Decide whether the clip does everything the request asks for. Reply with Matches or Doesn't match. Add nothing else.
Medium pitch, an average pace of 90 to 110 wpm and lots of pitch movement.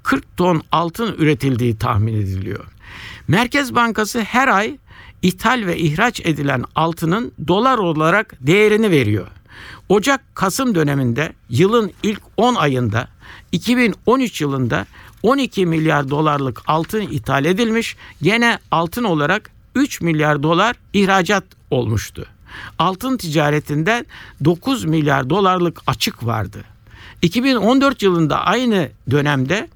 Matches